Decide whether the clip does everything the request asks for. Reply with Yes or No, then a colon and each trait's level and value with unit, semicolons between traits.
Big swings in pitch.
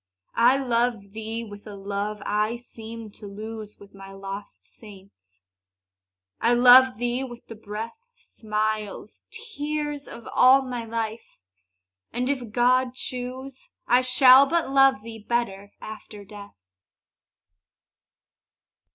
No: average, 3.3 semitones